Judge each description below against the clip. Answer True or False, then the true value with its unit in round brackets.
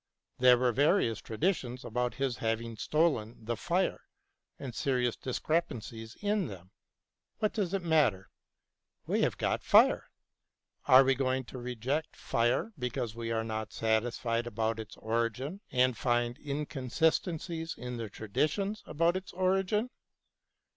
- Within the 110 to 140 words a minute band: True (135 wpm)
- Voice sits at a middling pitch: False (125 Hz)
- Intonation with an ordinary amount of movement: False (5.9 semitones)